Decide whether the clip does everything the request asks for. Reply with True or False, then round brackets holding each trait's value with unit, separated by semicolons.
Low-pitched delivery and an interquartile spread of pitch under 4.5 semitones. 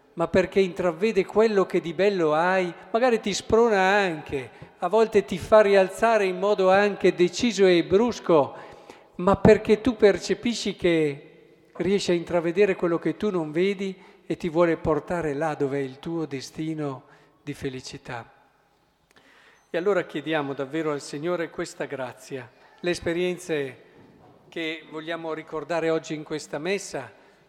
False (175 Hz; 3.9 semitones)